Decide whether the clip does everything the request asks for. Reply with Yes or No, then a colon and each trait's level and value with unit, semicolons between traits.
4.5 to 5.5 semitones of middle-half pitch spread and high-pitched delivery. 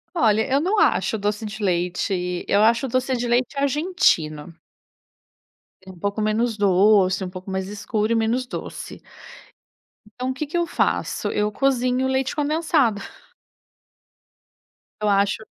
Yes: average, 4.8 semitones; high, 220 Hz